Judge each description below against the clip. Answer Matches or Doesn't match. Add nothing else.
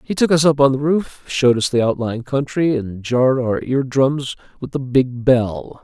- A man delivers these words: Matches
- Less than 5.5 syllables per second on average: Matches